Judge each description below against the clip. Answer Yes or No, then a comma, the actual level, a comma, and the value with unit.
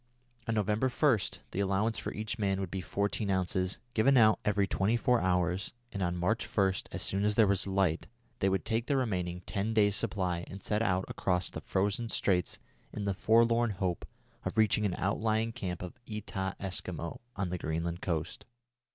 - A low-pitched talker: Yes, low, 100 Hz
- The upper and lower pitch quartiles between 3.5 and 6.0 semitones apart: No, average, 3.0 semitones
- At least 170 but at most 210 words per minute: Yes, average, 185 wpm